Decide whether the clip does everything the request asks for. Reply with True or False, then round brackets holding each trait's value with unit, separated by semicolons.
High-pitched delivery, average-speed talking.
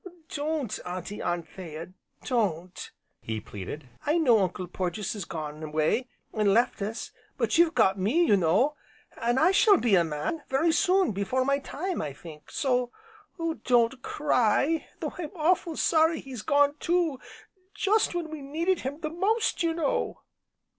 True (255 Hz; 160 wpm)